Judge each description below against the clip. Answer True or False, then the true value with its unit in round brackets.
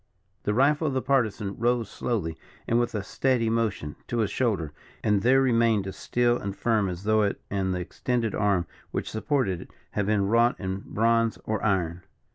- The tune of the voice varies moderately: True (3.5 semitones)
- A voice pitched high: False (110 Hz)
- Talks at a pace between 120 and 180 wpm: False (190 wpm)